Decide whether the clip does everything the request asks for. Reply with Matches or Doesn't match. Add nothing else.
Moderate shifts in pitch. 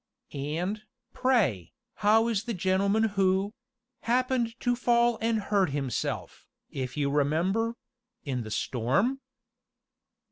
Doesn't match